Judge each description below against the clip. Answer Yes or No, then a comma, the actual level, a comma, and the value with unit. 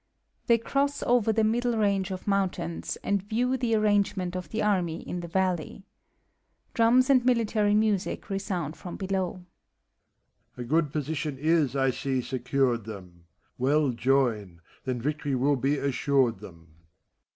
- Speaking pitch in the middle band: Yes, medium, 175 Hz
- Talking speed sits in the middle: Yes, average, 145 wpm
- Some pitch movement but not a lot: No, wide, 7.6 semitones